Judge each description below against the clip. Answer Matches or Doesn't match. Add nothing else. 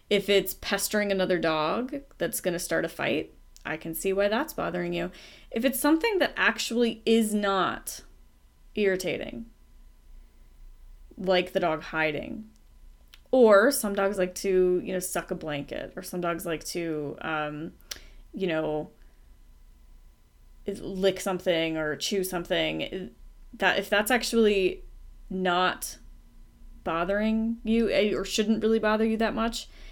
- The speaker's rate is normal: Doesn't match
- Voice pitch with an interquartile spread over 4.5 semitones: Matches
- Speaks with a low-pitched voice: Doesn't match